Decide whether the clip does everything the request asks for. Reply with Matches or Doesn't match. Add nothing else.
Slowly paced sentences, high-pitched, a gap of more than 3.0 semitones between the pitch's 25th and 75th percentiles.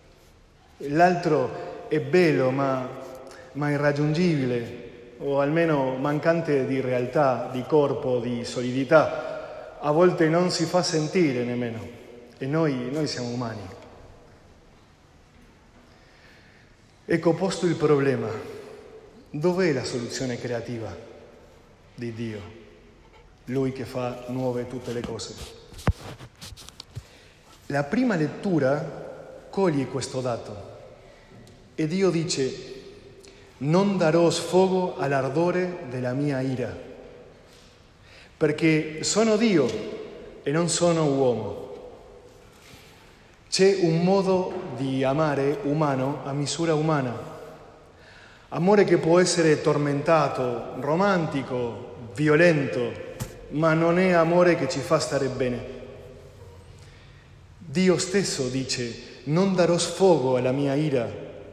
Doesn't match